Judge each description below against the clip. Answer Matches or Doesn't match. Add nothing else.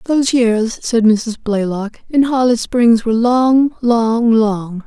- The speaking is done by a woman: Matches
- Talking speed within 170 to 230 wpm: Doesn't match